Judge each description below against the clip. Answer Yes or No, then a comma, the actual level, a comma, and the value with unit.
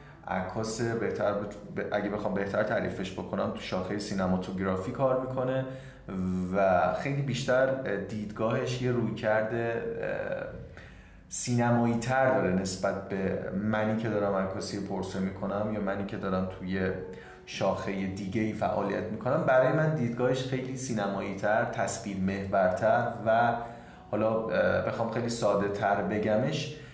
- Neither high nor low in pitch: No, low, 105 Hz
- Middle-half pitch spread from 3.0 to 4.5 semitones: Yes, average, 3.6 semitones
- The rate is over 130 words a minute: No, average, 125 wpm